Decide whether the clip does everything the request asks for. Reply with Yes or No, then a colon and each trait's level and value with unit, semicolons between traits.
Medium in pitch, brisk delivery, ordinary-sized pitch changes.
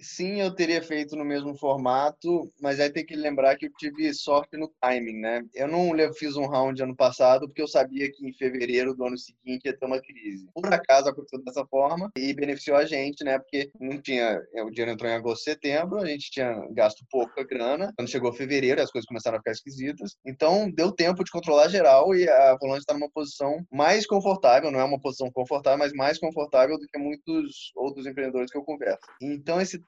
Yes: medium, 145 Hz; fast, 215 wpm; average, 3.0 semitones